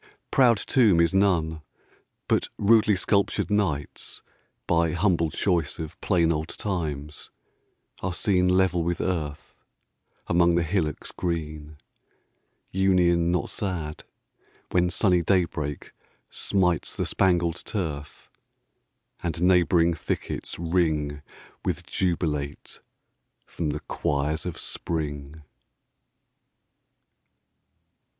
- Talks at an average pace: No, slow, 100 wpm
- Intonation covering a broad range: No, average, 3.0 semitones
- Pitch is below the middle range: Yes, very low, 85 Hz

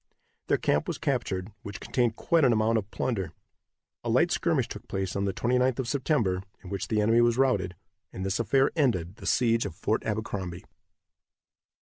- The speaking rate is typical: Yes, average, 180 wpm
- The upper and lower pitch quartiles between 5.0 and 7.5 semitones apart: No, average, 4.2 semitones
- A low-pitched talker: Yes, low, 110 Hz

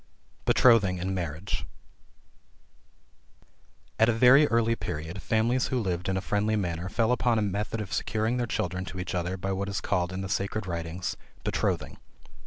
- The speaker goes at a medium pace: Yes, average, 170 wpm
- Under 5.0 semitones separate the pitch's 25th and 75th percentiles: Yes, average, 3.6 semitones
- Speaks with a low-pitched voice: Yes, low, 100 Hz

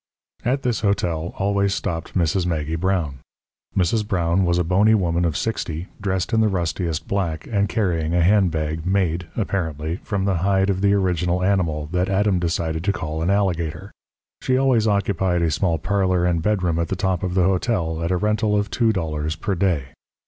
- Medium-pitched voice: No, very low, 90 Hz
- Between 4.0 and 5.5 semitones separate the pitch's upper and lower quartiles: No, average, 3.2 semitones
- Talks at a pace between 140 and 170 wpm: No, average, 185 wpm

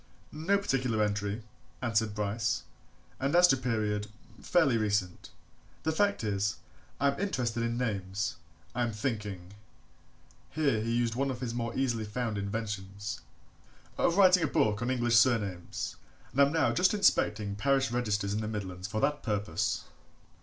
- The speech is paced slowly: No, average, 155 wpm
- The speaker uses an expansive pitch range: No, average, 4.5 semitones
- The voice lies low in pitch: Yes, low, 115 Hz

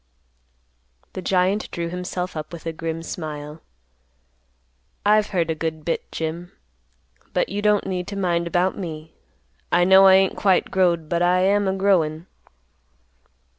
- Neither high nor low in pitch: Yes, medium, 175 Hz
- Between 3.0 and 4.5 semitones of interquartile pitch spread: No, narrow, 2.6 semitones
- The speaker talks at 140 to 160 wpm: Yes, average, 150 wpm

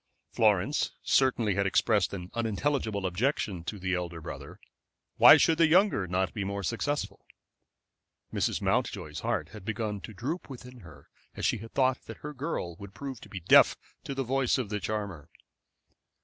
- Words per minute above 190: No, average, 165 wpm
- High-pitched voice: No, low, 110 Hz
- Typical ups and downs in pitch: No, wide, 5.8 semitones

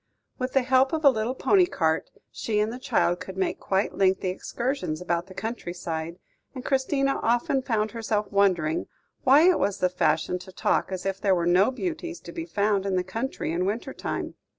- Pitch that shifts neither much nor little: No, wide, 6.2 semitones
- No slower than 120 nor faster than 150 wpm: No, average, 200 wpm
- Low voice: No, high, 210 Hz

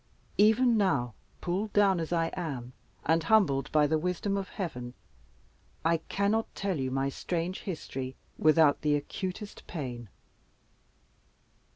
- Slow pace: Yes, slow, 130 wpm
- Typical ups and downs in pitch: No, wide, 5.9 semitones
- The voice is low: No, medium, 165 Hz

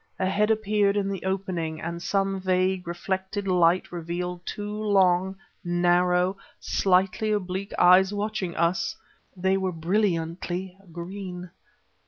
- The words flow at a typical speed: No, slow, 120 wpm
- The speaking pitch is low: No, medium, 185 Hz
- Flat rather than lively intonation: Yes, narrow, 1.8 semitones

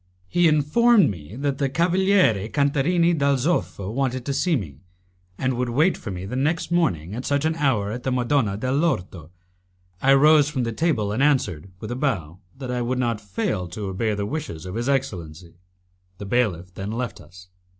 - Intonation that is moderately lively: No, wide, 6.4 semitones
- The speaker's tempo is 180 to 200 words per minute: Yes, average, 190 wpm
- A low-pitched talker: Yes, low, 125 Hz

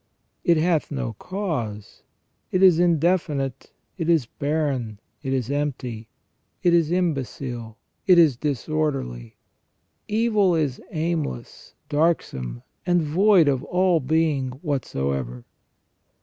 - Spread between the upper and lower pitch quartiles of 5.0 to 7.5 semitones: Yes, wide, 5.4 semitones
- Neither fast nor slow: No, slow, 105 wpm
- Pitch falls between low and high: Yes, medium, 150 Hz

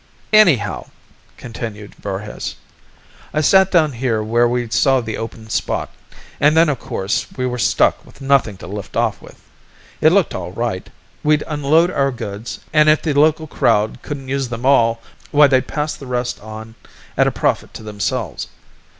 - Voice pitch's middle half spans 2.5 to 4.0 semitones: No, average, 5.1 semitones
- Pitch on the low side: Yes, low, 125 Hz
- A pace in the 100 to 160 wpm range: No, average, 170 wpm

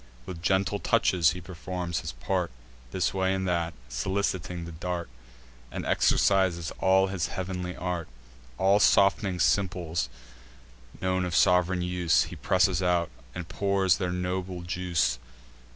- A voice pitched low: Yes, very low, 90 Hz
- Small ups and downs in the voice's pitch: Yes, narrow, 1.6 semitones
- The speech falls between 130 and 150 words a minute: Yes, slow, 135 wpm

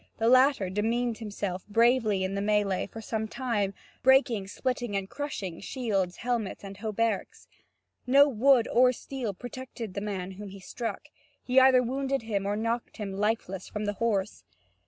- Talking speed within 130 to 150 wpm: No, average, 160 wpm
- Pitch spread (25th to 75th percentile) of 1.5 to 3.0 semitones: No, average, 3.9 semitones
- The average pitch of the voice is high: Yes, high, 220 Hz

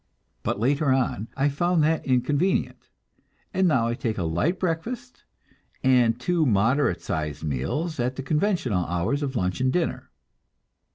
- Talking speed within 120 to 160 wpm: Yes, average, 150 wpm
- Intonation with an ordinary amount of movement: No, wide, 6.1 semitones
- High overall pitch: No, low, 130 Hz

